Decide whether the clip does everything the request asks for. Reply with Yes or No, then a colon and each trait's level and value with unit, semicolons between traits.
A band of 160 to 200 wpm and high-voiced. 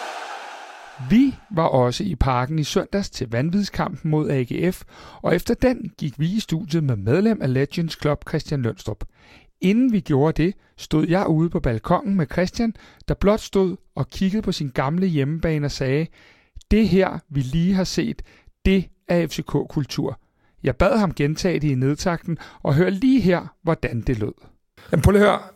No: average, 170 wpm; medium, 165 Hz